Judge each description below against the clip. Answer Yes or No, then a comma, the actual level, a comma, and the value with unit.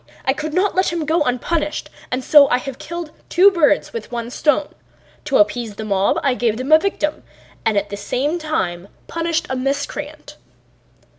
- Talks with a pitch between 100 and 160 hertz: No, very high, 290 Hz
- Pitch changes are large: No, average, 4.9 semitones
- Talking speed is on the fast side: No, average, 180 wpm